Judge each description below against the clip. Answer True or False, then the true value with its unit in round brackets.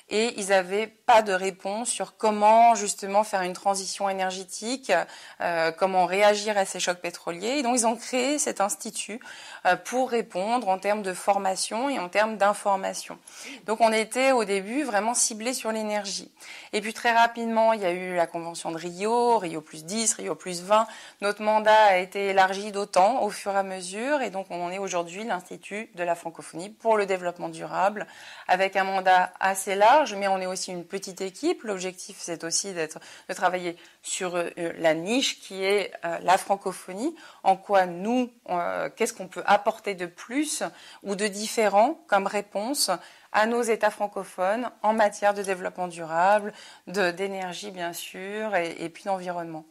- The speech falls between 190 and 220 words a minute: False (175 wpm)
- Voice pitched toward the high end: True (200 Hz)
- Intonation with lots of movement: False (3.1 semitones)